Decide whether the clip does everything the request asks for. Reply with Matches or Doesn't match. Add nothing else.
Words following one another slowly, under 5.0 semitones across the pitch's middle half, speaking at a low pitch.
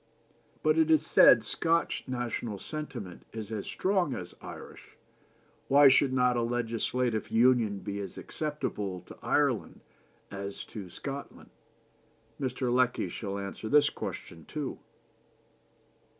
Doesn't match